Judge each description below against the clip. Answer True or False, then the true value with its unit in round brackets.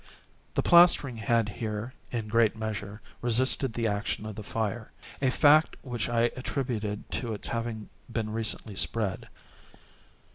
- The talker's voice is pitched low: True (115 Hz)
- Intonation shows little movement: True (2.1 semitones)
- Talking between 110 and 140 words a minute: True (135 wpm)